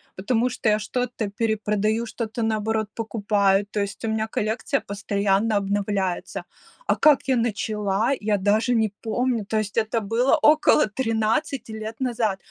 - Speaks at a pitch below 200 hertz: No, high, 220 Hz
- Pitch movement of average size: No, narrow, 2.0 semitones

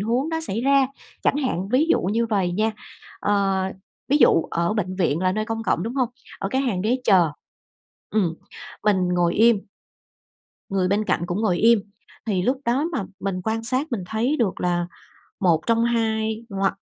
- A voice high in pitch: Yes, high, 215 Hz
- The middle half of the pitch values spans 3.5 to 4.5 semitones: Yes, average, 4.1 semitones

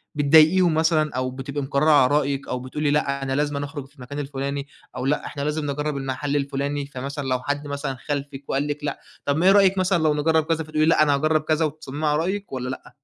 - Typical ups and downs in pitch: No, narrow, 1.9 semitones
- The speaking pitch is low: No, medium, 145 Hz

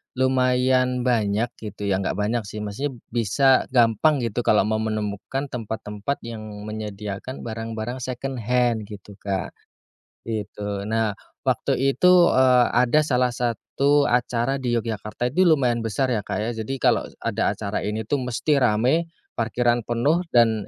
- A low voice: Yes, low, 120 Hz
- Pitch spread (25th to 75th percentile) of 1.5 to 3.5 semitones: Yes, average, 3.0 semitones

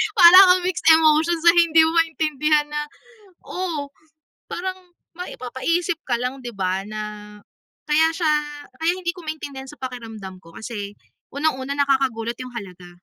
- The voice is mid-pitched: No, very high, 285 Hz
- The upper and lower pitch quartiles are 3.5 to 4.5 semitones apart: No, average, 5.3 semitones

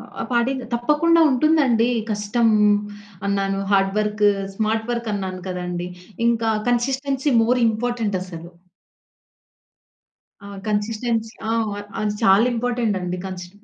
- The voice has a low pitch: No, high, 225 Hz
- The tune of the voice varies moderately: Yes, average, 3.6 semitones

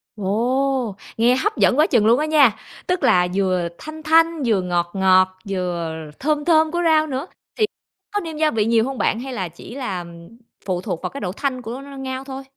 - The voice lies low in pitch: No, very high, 255 Hz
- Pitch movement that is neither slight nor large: No, wide, 8.0 semitones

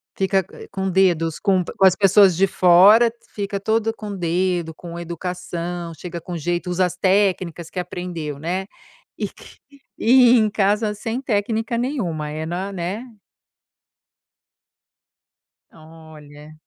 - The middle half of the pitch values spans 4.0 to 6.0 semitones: No, average, 3.2 semitones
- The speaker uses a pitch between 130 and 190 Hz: Yes, medium, 185 Hz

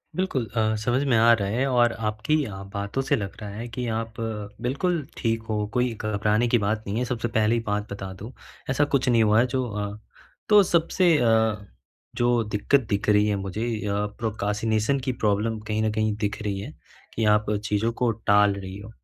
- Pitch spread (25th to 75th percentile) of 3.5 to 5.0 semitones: No, average, 2.7 semitones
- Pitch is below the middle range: Yes, low, 110 Hz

